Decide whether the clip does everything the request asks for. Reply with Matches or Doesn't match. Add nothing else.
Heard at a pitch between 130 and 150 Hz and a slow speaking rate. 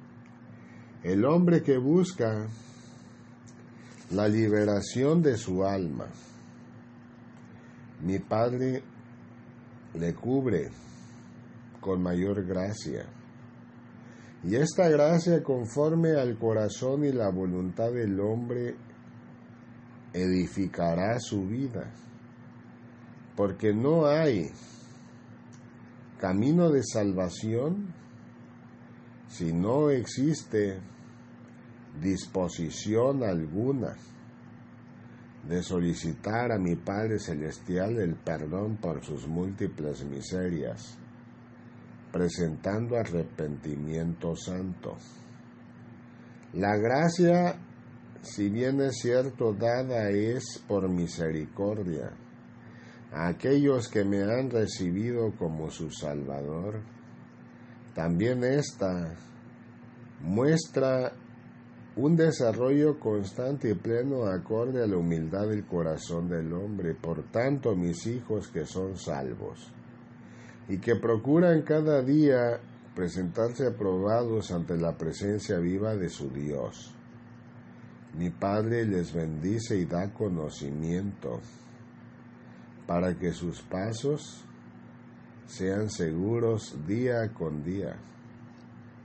Doesn't match